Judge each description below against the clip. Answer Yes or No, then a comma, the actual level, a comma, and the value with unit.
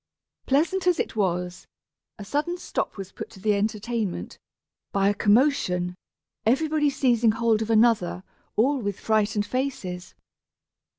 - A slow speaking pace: Yes, slow, 130 wpm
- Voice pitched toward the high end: Yes, high, 220 Hz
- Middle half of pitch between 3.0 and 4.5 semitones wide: No, average, 5.1 semitones